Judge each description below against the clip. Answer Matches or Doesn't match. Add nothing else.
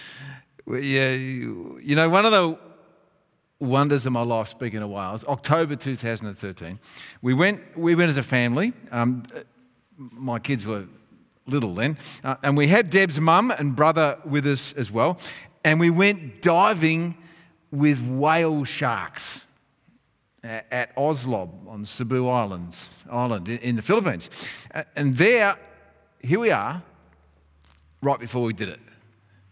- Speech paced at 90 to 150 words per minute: Matches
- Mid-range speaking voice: Doesn't match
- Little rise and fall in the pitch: Doesn't match